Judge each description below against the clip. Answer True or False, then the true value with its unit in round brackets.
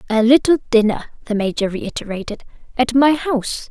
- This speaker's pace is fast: False (145 wpm)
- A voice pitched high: True (235 Hz)